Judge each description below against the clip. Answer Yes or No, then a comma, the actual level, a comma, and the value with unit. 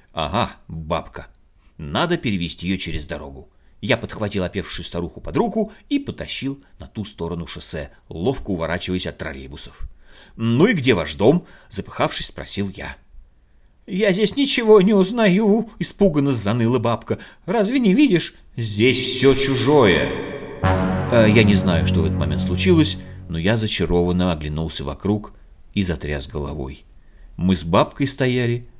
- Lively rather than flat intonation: Yes, wide, 7.9 semitones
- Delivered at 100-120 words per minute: No, average, 135 wpm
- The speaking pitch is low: Yes, very low, 95 Hz